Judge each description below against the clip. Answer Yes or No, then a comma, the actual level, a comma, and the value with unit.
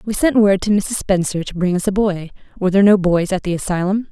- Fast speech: Yes, fast, 265 wpm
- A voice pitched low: No, high, 195 Hz